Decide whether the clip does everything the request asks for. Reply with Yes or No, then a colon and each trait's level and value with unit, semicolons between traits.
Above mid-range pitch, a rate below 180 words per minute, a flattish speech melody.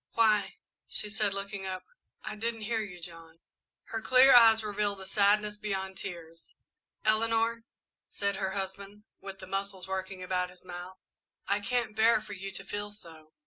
Yes: high, 200 Hz; average, 165 wpm; narrow, 2.3 semitones